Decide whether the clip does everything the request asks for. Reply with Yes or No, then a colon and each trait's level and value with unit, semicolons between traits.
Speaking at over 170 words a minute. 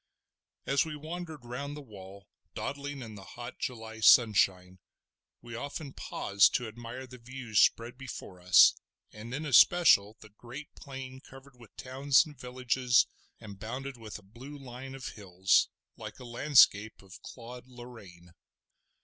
No: average, 150 wpm